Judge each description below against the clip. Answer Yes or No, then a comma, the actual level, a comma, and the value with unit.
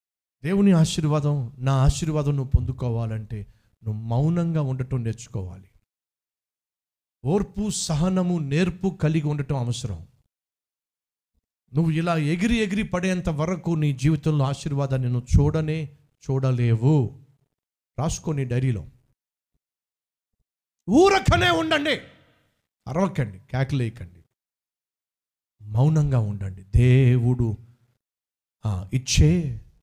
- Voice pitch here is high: No, low, 135 Hz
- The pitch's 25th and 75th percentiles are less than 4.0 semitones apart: No, average, 5.1 semitones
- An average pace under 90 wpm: Yes, average, 75 wpm